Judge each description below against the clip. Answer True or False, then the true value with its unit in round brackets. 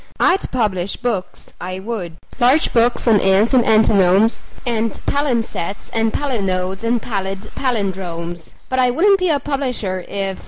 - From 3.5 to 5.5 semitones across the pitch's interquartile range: True (4.5 semitones)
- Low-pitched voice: False (220 Hz)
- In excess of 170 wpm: False (145 wpm)